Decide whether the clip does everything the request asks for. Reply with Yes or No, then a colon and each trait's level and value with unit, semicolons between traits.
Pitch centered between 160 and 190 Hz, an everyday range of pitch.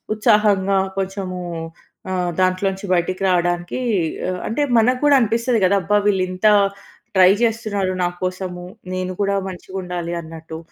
No: medium, 185 Hz; narrow, 2.3 semitones